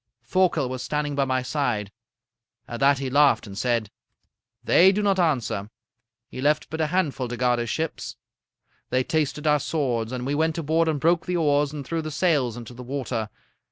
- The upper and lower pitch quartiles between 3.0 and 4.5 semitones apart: Yes, average, 4.2 semitones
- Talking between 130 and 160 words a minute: No, average, 195 wpm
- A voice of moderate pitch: Yes, medium, 145 Hz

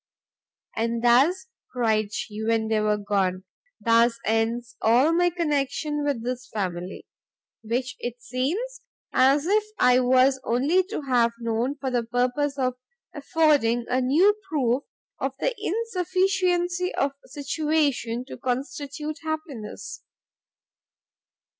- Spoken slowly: Yes, slow, 120 wpm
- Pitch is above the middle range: Yes, very high, 255 Hz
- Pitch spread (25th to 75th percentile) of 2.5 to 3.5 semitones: No, average, 4.9 semitones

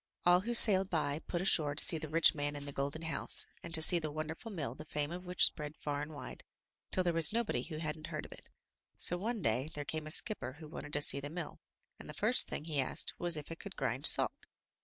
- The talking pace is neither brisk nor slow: No, fast, 255 wpm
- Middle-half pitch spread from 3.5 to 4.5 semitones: No, average, 3.1 semitones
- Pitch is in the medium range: Yes, medium, 155 Hz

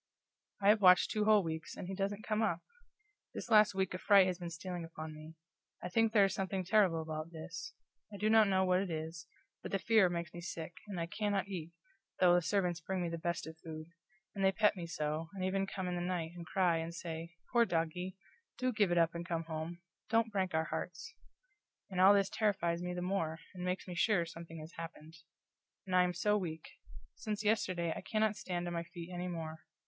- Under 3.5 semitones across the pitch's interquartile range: Yes, average, 2.9 semitones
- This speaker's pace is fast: Yes, fast, 225 wpm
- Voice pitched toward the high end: No, medium, 180 Hz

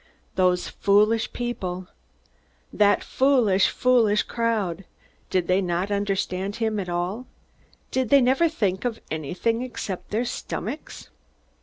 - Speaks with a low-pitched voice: No, high, 205 Hz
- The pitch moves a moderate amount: Yes, average, 4.5 semitones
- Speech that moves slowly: Yes, slow, 120 wpm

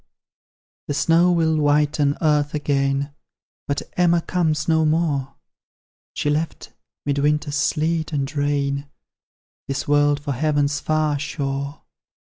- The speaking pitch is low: No, medium, 145 Hz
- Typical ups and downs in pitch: No, narrow, 1.7 semitones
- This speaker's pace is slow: Yes, slow, 115 wpm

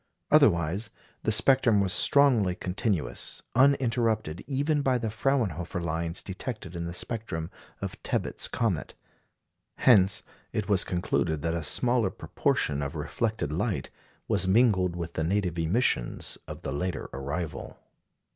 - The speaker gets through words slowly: Yes, slow, 130 wpm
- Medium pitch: No, very low, 95 Hz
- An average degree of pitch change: No, wide, 5.7 semitones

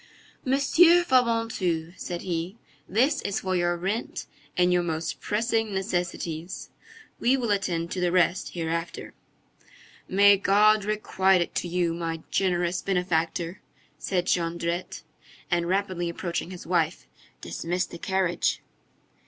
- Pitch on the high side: No, medium, 180 Hz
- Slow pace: Yes, slow, 125 wpm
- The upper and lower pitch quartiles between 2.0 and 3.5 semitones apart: Yes, average, 2.9 semitones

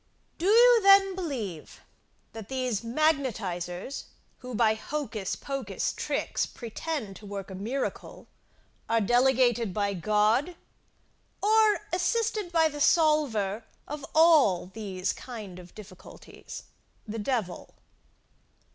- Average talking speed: No, slow, 110 wpm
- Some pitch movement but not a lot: No, wide, 7.3 semitones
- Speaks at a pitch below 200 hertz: No, high, 240 Hz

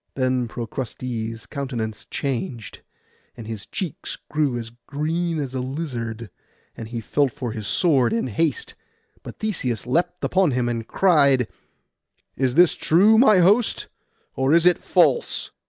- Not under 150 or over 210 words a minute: No, average, 140 wpm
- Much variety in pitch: Yes, wide, 6.2 semitones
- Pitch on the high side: No, low, 130 Hz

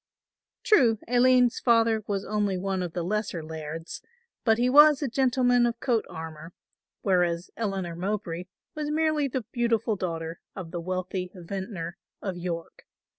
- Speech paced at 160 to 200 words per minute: No, average, 145 wpm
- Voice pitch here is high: Yes, high, 200 Hz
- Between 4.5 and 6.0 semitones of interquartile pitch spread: Yes, wide, 5.6 semitones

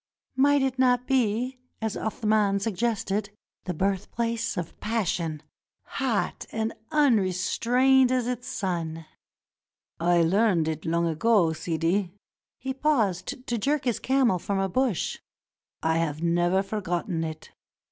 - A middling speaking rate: No, slow, 130 wpm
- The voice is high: Yes, high, 205 Hz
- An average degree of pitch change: No, wide, 6.2 semitones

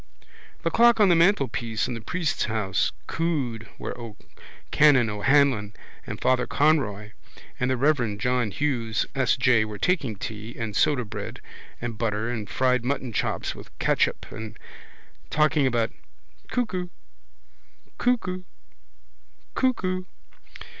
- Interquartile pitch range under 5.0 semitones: No, wide, 5.6 semitones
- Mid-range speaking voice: No, low, 125 Hz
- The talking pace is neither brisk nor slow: No, slow, 120 wpm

